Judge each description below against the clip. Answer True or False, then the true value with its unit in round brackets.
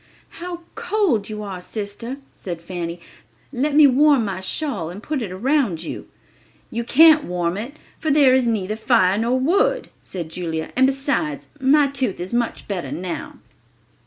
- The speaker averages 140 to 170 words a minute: True (160 wpm)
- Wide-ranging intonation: True (7.3 semitones)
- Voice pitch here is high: True (235 Hz)